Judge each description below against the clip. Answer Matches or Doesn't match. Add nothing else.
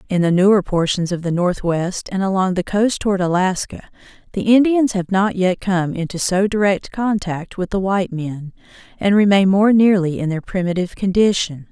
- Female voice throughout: Matches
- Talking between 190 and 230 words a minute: Doesn't match